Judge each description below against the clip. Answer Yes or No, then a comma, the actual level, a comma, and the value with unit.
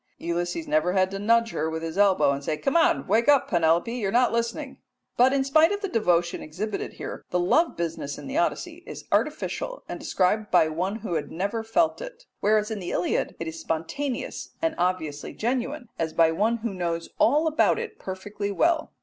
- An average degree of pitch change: No, wide, 7.8 semitones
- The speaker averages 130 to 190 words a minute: No, average, 200 wpm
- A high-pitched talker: Yes, high, 210 Hz